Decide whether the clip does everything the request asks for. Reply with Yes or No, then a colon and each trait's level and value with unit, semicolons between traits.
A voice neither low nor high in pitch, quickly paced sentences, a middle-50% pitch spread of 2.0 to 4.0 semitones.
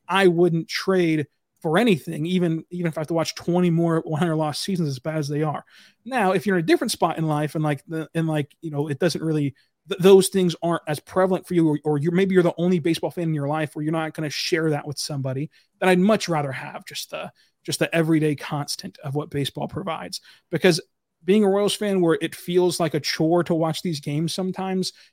Yes: medium, 165 Hz; fast, 240 wpm; average, 2.9 semitones